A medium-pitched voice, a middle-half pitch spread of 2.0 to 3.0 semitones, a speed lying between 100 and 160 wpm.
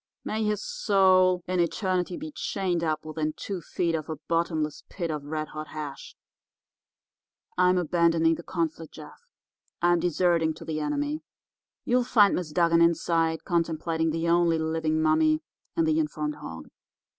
Yes: medium, 170 Hz; average, 2.7 semitones; average, 150 wpm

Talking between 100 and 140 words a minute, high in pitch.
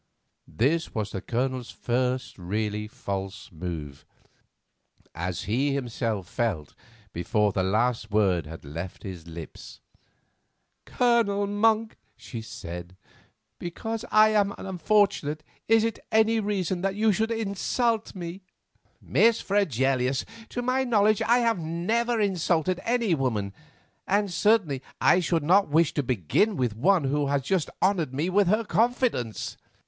No: slow, 135 wpm; medium, 160 Hz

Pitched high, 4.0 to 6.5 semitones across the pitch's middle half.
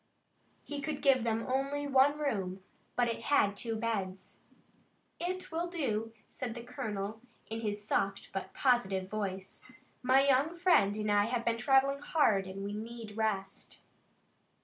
Yes: high, 230 Hz; average, 5.0 semitones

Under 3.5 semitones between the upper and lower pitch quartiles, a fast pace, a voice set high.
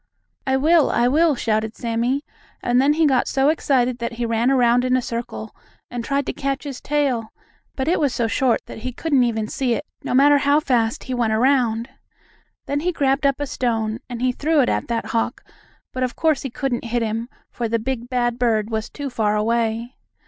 Yes: average, 3.1 semitones; fast, 215 wpm; high, 245 Hz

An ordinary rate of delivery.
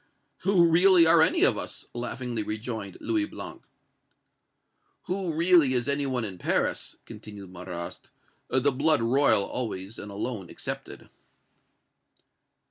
No: slow, 130 wpm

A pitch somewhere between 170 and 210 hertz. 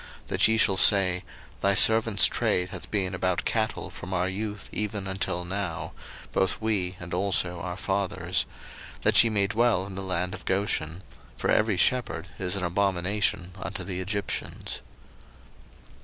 No: very low, 95 Hz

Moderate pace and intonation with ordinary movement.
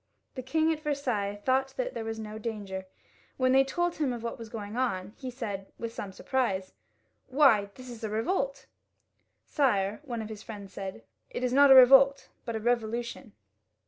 Yes: average, 190 wpm; average, 4.2 semitones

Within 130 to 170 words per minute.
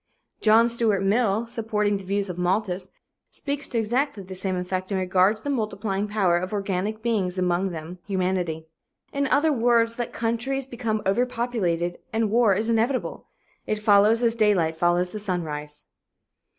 Yes: average, 160 wpm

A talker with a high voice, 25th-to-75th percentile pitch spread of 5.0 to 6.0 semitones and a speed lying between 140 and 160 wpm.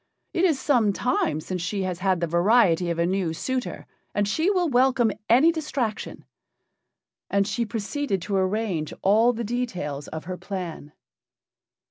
Yes: high, 205 Hz; wide, 5.4 semitones; average, 155 wpm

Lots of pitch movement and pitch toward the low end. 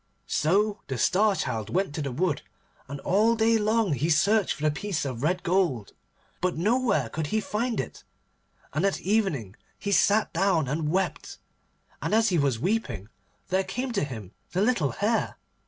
No: wide, 6.2 semitones; medium, 185 Hz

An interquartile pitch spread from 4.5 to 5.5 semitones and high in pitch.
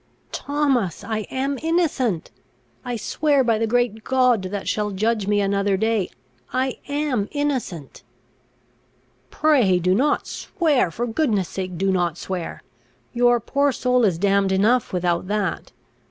Yes: average, 5.2 semitones; high, 225 Hz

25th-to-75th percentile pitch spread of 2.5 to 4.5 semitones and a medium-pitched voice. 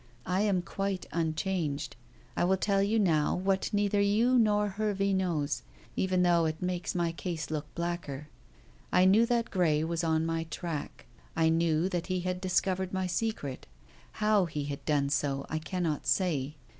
Yes: average, 3.6 semitones; medium, 175 Hz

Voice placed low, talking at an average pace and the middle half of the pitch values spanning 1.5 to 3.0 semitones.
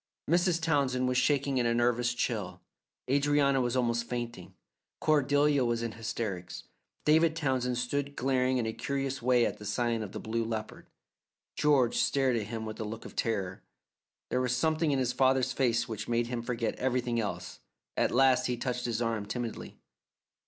Yes: low, 125 Hz; average, 175 wpm; narrow, 2.5 semitones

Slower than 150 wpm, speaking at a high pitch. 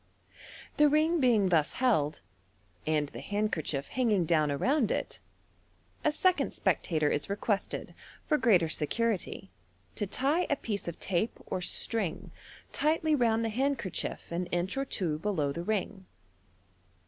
Yes: slow, 135 wpm; high, 205 Hz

